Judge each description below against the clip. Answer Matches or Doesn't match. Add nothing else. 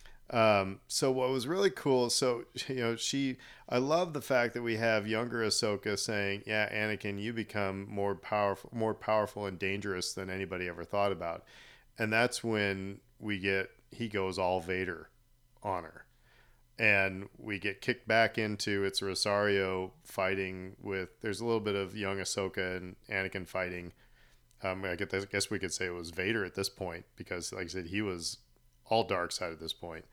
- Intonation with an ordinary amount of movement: Matches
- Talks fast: Doesn't match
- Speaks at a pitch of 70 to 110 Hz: Matches